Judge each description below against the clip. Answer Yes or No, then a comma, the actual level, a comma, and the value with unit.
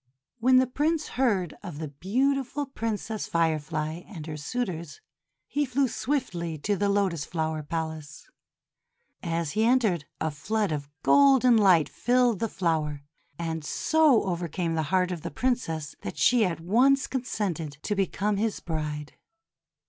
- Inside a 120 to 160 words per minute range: Yes, average, 150 wpm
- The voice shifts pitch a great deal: Yes, wide, 7.2 semitones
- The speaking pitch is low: No, medium, 185 Hz